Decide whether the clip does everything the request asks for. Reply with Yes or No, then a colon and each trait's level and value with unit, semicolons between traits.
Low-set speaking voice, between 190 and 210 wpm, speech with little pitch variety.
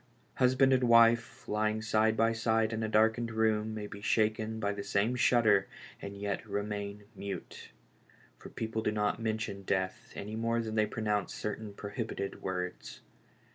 No: low, 110 Hz; average, 160 wpm; narrow, 1.8 semitones